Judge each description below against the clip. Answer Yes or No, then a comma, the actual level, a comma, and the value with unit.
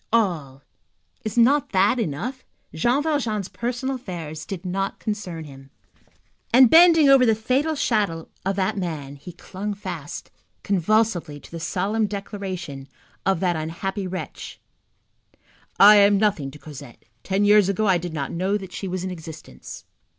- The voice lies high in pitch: Yes, high, 195 Hz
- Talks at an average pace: Yes, average, 150 wpm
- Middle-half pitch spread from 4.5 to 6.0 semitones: Yes, average, 4.8 semitones